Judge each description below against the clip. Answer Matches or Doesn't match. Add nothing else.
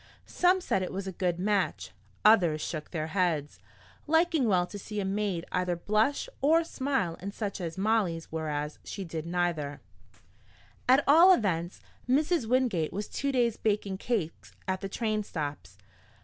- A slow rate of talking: Doesn't match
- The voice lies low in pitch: Doesn't match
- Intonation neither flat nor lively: Doesn't match